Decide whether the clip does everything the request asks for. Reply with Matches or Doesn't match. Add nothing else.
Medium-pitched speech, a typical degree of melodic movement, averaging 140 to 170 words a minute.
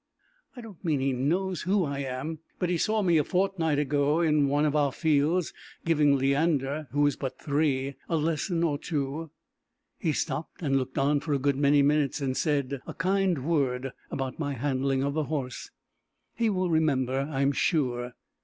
Doesn't match